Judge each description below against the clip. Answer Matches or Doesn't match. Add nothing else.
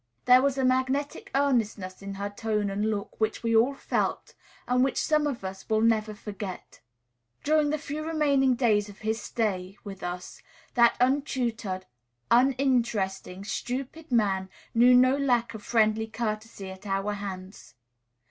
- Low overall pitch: Doesn't match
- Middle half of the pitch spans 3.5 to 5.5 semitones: Matches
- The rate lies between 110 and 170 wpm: Matches